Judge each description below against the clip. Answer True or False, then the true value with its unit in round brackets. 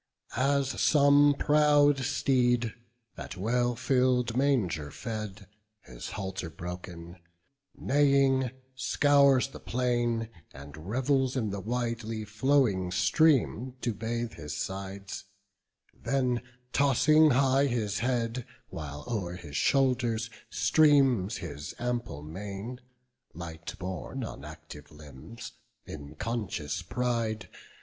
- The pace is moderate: False (105 wpm)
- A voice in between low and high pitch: False (115 Hz)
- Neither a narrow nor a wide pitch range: False (5.8 semitones)